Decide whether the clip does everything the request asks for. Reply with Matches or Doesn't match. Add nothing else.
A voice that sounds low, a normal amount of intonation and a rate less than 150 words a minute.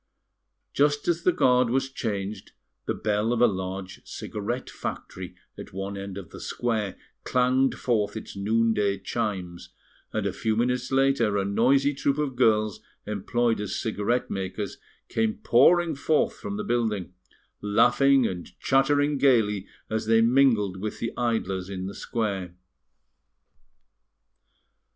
Matches